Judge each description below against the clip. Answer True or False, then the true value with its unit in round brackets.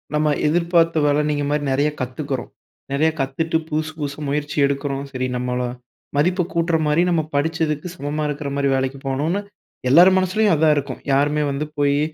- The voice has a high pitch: False (150 Hz)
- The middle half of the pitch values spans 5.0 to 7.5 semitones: False (2.5 semitones)